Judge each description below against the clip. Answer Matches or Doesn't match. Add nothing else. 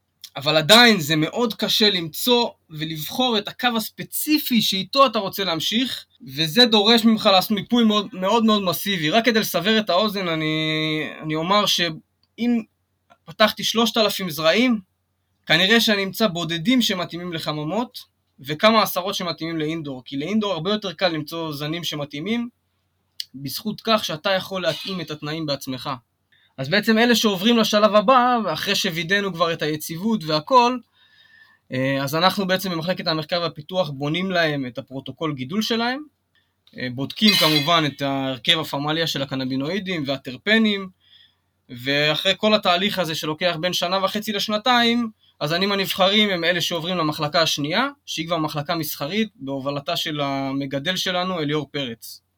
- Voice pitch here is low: Doesn't match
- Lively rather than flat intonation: Matches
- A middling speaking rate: Matches